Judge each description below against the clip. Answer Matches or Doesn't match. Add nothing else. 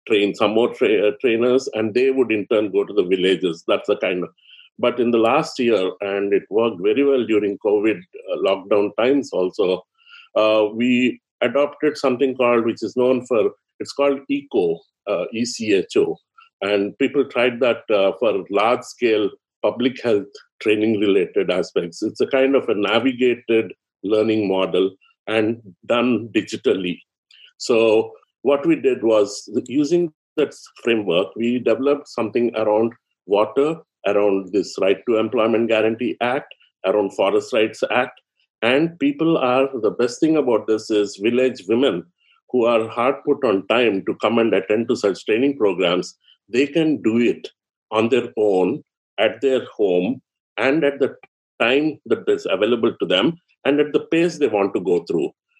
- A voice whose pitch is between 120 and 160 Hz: Matches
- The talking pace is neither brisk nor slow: Matches